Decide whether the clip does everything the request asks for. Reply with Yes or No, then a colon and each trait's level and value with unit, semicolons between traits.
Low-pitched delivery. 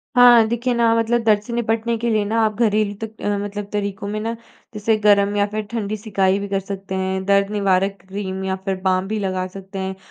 No: high, 205 Hz